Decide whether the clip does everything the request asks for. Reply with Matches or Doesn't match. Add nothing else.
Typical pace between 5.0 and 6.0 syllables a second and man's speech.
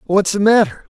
Matches